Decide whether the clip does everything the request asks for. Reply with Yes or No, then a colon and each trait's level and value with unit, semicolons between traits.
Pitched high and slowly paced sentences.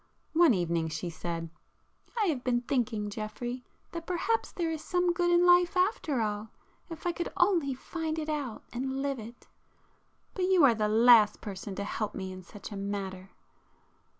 No: high, 245 Hz; average, 175 wpm